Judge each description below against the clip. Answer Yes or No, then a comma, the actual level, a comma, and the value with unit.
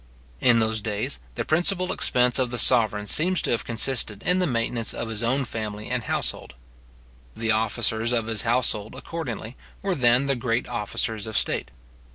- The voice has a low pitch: Yes, low, 115 Hz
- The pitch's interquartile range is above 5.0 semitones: No, average, 2.7 semitones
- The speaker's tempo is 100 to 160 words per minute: No, average, 175 wpm